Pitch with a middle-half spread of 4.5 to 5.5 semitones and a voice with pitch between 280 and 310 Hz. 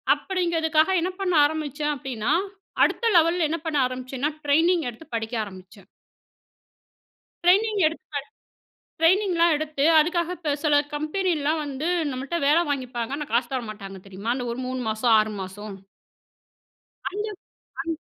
Yes: average, 5.2 semitones; very high, 295 Hz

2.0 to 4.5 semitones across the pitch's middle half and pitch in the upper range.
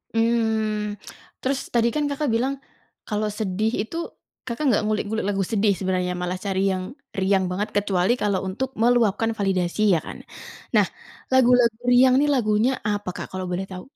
Yes: average, 3.6 semitones; high, 215 Hz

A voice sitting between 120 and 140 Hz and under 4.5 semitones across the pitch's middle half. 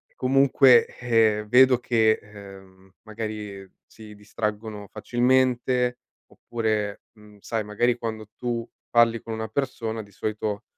No: low, 110 Hz; narrow, 2.4 semitones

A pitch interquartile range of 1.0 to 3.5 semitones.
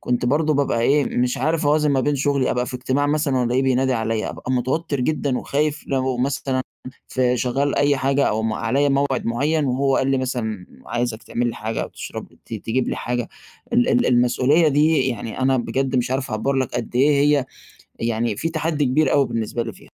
Yes: average, 2.7 semitones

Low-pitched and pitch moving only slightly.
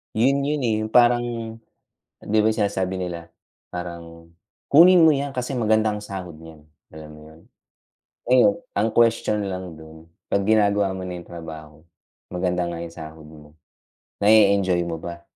No: very low, 95 Hz; average, 4.7 semitones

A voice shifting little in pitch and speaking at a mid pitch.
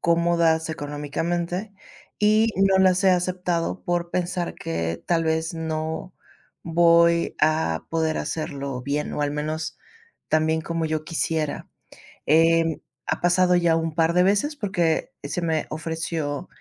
Yes: narrow, 1.9 semitones; medium, 165 Hz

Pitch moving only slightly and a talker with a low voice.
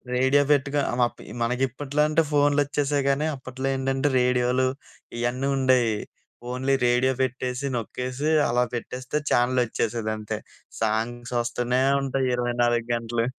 Yes: narrow, 1.9 semitones; low, 125 Hz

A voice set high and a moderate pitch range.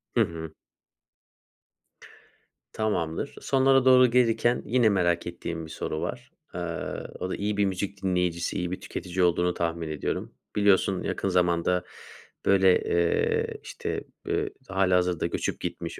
No: very low, 90 Hz; average, 3.1 semitones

